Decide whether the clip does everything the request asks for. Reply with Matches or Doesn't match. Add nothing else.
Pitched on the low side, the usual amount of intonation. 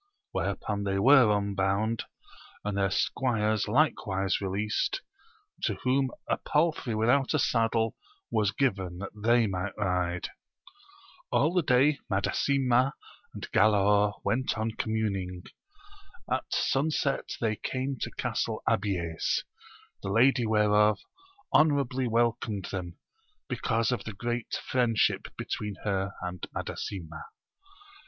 Matches